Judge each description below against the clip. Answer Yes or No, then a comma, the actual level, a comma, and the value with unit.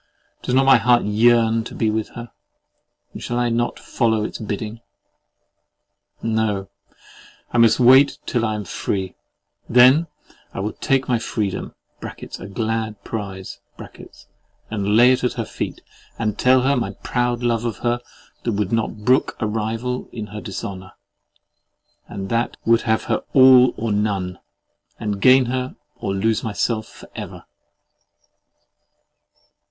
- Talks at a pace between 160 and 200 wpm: No, average, 145 wpm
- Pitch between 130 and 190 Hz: No, low, 115 Hz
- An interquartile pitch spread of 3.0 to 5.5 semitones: No, narrow, 2.6 semitones